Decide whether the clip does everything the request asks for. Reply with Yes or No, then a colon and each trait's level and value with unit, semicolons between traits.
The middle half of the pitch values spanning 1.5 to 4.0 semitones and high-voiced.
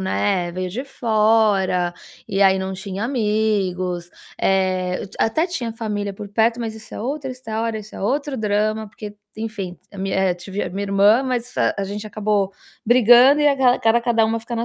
Yes: average, 3.2 semitones; high, 215 Hz